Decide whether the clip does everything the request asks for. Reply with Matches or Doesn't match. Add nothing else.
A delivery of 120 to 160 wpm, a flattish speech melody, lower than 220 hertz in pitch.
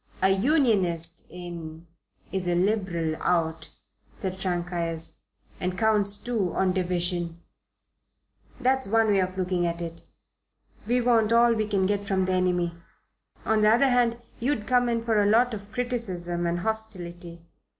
Doesn't match